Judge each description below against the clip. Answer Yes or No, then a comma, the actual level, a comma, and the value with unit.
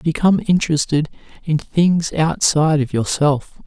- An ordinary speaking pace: No, slow, 115 wpm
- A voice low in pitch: No, medium, 155 Hz